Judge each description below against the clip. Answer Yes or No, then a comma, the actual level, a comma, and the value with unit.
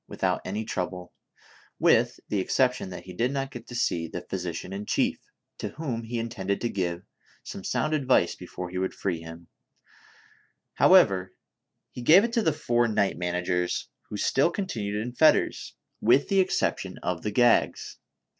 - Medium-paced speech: Yes, average, 165 wpm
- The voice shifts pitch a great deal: Yes, wide, 5.7 semitones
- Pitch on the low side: Yes, low, 105 Hz